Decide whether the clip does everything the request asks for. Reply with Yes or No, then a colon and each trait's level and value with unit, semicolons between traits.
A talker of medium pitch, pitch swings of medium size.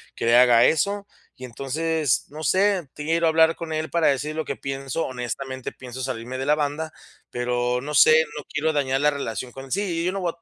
Yes: medium, 145 Hz; average, 3.8 semitones